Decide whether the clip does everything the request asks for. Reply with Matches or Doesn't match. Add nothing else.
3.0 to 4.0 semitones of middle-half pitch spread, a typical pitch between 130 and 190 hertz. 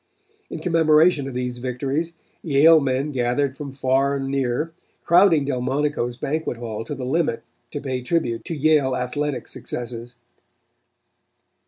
Matches